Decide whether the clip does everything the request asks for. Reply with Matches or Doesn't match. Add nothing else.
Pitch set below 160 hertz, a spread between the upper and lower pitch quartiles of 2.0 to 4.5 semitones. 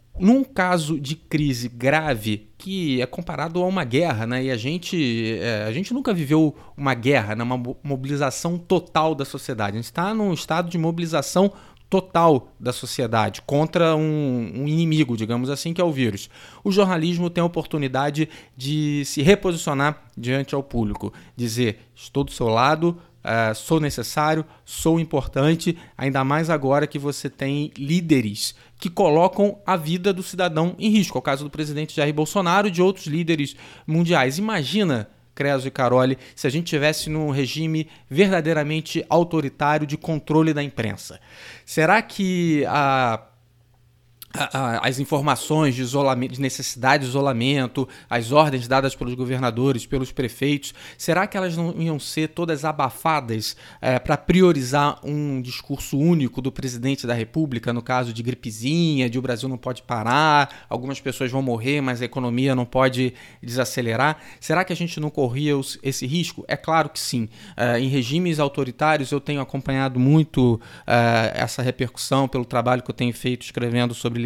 Matches